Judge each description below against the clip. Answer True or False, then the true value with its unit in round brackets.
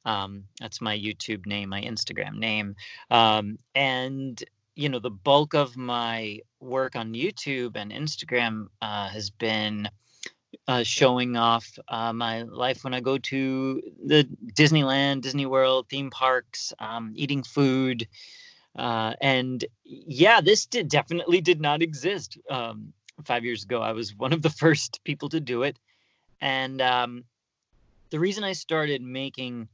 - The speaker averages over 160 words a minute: False (145 wpm)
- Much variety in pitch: False (3.6 semitones)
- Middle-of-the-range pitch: False (125 Hz)